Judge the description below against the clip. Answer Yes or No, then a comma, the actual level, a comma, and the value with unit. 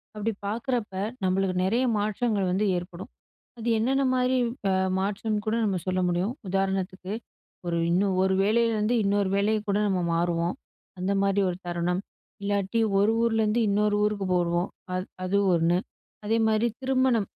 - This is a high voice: Yes, high, 200 Hz